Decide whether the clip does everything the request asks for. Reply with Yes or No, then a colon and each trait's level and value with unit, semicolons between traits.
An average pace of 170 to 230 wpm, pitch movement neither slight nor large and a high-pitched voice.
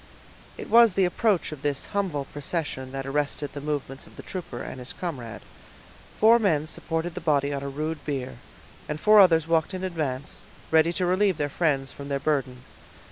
No: average, 190 wpm; average, 4.2 semitones; medium, 150 Hz